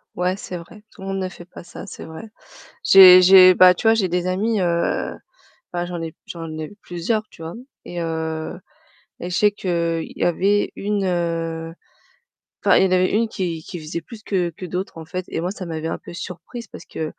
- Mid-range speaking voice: Yes, medium, 180 Hz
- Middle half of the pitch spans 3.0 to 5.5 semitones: No, narrow, 2.4 semitones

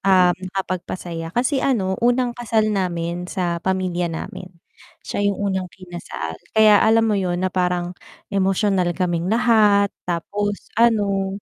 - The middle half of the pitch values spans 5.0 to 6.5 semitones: No, average, 2.9 semitones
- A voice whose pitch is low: No, high, 190 Hz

